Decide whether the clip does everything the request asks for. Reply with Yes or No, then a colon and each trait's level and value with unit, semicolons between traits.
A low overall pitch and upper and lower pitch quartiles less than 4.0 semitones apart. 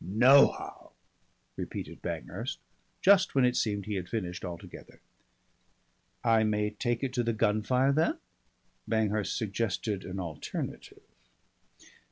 Yes: low, 110 Hz; average, 3.6 semitones